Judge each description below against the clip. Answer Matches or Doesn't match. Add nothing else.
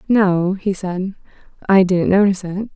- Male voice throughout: Doesn't match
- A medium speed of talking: Matches